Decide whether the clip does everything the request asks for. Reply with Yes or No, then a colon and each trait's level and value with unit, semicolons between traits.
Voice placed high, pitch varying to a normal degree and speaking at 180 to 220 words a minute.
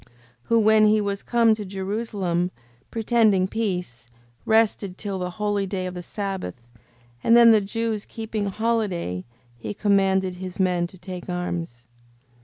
No: high, 195 Hz; average, 3.3 semitones; average, 150 wpm